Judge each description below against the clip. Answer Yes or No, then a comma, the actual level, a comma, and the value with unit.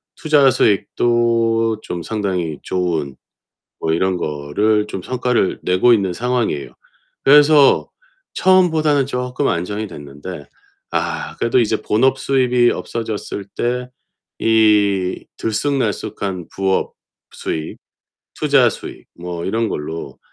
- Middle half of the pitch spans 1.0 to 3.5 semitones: No, wide, 5.4 semitones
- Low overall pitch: Yes, low, 110 Hz